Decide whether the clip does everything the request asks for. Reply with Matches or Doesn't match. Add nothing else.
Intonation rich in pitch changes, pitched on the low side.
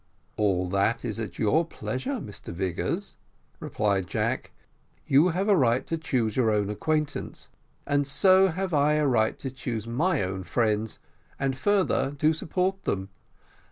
Matches